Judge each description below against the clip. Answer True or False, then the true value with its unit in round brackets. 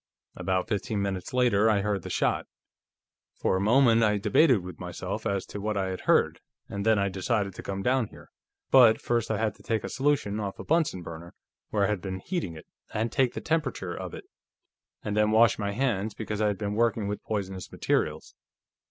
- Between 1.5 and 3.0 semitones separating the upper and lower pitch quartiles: True (2.7 semitones)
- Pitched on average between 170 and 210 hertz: False (105 Hz)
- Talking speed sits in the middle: False (210 wpm)